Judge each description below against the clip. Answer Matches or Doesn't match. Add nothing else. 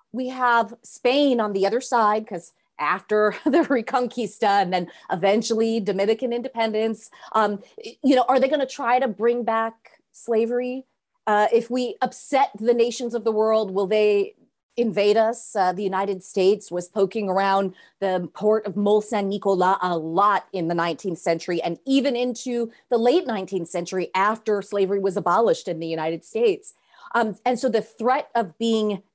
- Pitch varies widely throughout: Doesn't match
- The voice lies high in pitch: Matches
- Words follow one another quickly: Doesn't match